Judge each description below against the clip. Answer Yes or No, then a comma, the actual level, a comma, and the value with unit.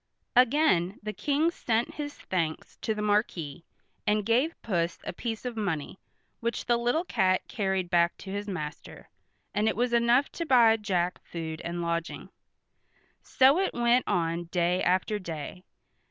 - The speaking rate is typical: Yes, average, 155 wpm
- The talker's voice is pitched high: Yes, high, 205 Hz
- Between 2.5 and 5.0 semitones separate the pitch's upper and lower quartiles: No, wide, 5.5 semitones